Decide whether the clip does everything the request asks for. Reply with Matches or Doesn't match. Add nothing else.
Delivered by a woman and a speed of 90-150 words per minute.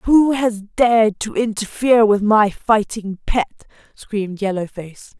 Matches